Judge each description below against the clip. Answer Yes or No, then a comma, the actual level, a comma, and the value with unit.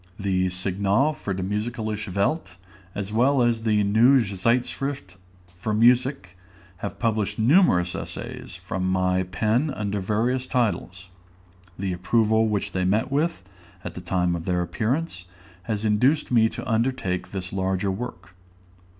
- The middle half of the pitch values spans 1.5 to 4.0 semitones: No, average, 4.4 semitones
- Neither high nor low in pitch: No, low, 105 Hz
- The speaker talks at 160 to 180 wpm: No, average, 140 wpm